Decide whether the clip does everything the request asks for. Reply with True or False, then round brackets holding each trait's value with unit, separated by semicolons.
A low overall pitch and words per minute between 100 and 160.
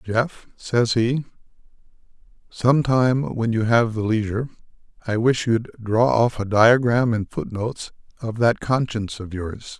True (115 Hz; 155 wpm)